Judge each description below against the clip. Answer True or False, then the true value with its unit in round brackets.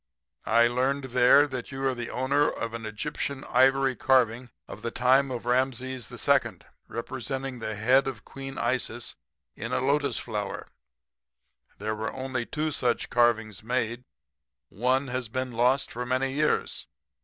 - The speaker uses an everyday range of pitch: False (2.2 semitones)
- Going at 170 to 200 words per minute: False (155 wpm)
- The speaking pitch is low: True (125 Hz)